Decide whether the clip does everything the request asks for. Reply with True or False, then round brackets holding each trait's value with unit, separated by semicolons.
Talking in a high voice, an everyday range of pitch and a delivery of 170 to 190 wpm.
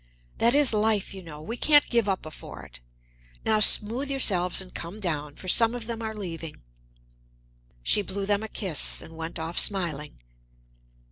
True (200 Hz; 5.0 semitones; 175 wpm)